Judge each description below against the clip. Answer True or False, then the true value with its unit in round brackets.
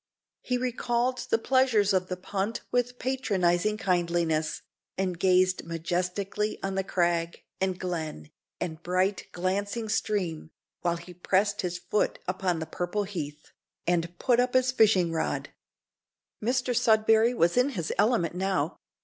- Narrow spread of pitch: False (4.2 semitones)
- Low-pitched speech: False (190 Hz)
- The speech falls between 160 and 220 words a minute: False (135 wpm)